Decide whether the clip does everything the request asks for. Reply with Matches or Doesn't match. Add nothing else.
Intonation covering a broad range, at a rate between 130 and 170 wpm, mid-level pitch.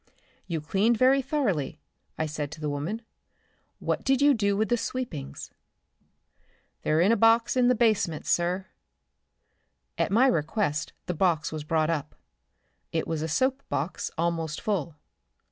Matches